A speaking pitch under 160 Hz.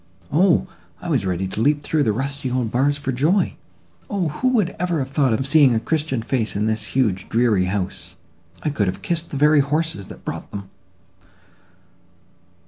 Yes: low, 135 Hz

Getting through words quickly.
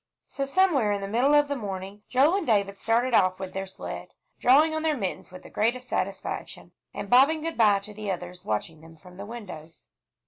Yes: fast, 210 wpm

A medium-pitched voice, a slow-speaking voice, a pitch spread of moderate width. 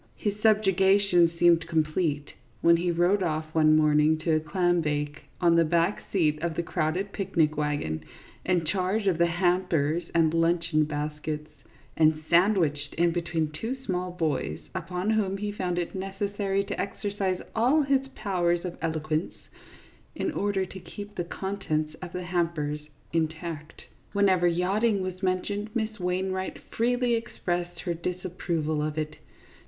No: medium, 175 Hz; average, 150 wpm; average, 3.6 semitones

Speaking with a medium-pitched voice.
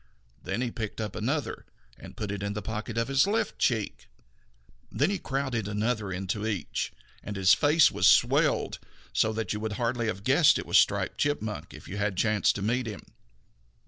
No: low, 110 Hz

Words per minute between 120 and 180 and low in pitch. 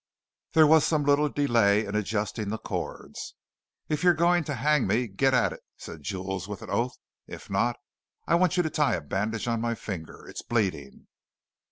No: average, 190 wpm; low, 120 Hz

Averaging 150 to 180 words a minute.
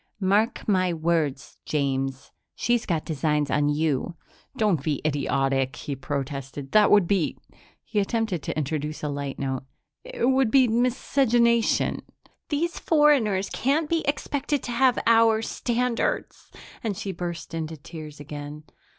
No: average, 140 wpm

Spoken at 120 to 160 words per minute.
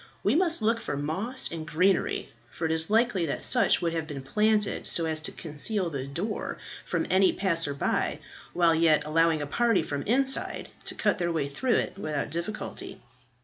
No: average, 190 wpm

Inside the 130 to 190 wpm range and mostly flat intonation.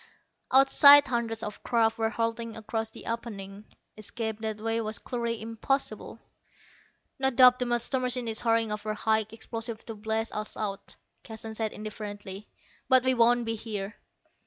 Yes: average, 155 wpm; narrow, 1.7 semitones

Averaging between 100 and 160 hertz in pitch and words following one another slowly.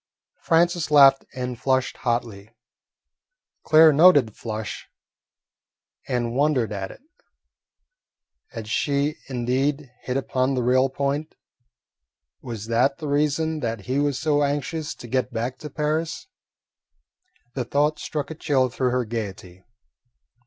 Yes: low, 135 Hz; slow, 125 wpm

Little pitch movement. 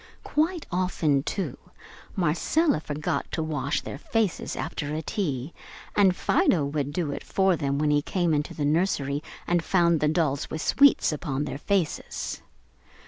No: average, 4.0 semitones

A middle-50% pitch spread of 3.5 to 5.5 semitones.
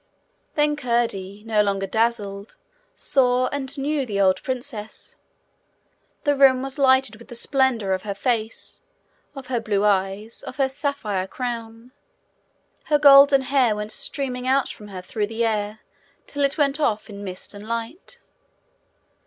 Yes: average, 4.5 semitones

